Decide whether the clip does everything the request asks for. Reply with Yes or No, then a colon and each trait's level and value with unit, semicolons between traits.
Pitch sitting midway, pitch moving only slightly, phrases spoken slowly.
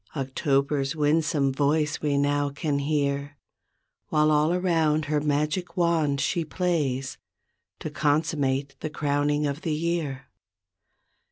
Yes: medium, 150 Hz; narrow, 1.8 semitones; slow, 115 wpm